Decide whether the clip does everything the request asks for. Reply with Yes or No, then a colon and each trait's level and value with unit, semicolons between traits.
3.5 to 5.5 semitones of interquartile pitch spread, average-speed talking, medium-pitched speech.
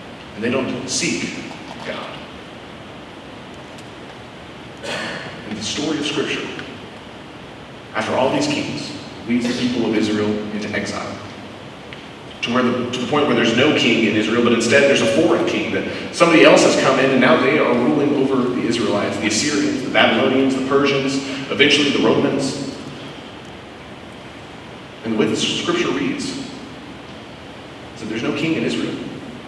No: average, 3.8 semitones; average, 155 wpm; low, 125 Hz